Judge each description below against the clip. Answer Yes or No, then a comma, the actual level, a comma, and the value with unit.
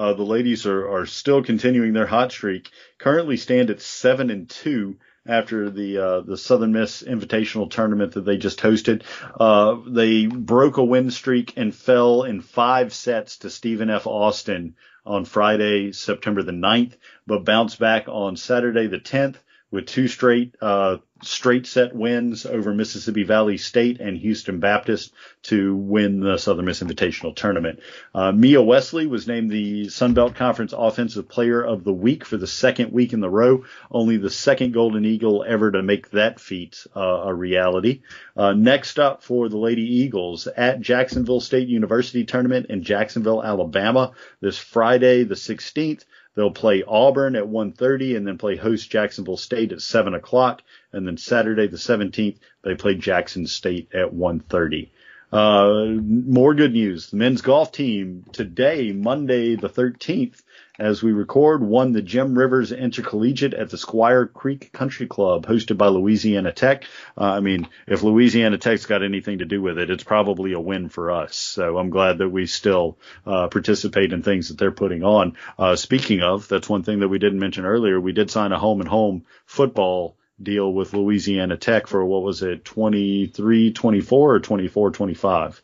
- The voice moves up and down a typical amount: Yes, average, 3.5 semitones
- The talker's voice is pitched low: Yes, low, 110 Hz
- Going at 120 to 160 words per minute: No, average, 170 wpm